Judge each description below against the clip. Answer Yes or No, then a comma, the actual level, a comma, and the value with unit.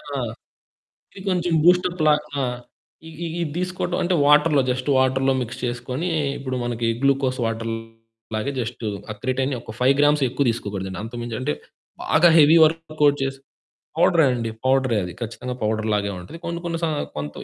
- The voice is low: Yes, low, 130 Hz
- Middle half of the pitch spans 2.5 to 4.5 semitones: No, average, 5.1 semitones